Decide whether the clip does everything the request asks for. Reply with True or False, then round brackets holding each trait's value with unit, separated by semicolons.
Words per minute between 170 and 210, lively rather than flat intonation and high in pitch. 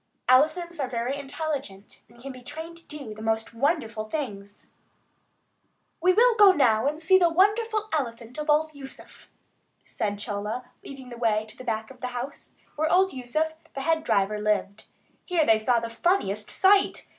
True (175 wpm; 6.3 semitones; 265 Hz)